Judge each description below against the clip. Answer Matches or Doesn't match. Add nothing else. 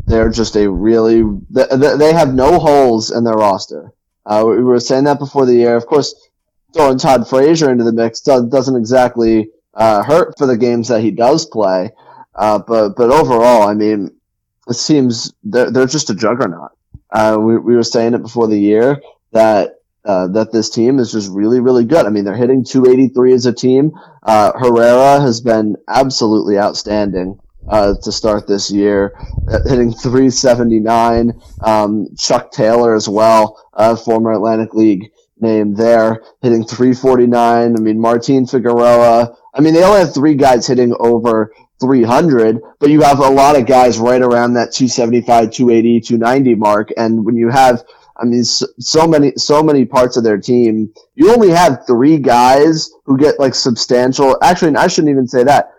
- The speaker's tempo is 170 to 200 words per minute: Matches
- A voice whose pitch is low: Matches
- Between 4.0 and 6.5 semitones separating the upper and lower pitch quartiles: Doesn't match